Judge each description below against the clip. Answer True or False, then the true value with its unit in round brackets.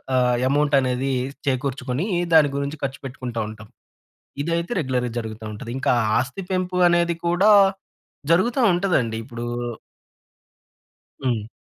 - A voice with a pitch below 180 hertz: True (135 Hz)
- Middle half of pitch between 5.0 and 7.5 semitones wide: True (5.4 semitones)